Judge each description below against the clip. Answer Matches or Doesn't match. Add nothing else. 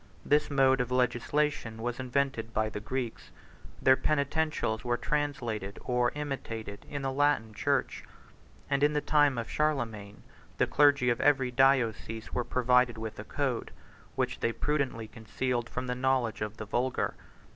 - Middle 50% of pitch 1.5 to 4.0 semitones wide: Matches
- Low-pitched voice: Matches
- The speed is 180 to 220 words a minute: Doesn't match